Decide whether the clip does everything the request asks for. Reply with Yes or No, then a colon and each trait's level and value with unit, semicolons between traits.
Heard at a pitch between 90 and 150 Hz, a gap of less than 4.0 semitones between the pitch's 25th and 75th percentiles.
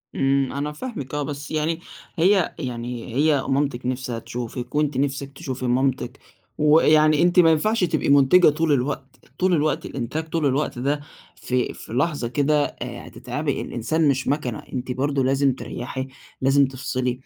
Yes: medium, 140 Hz; average, 3.0 semitones